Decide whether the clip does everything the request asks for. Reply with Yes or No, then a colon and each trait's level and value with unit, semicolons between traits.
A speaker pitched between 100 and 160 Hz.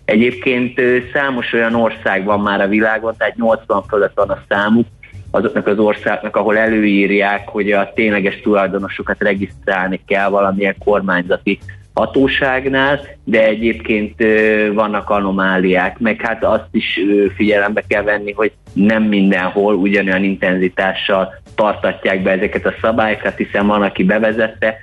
Yes: low, 105 Hz